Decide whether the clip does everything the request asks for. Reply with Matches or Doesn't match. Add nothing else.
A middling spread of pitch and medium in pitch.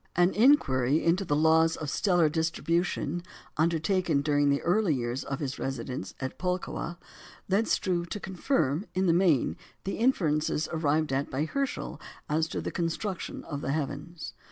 Matches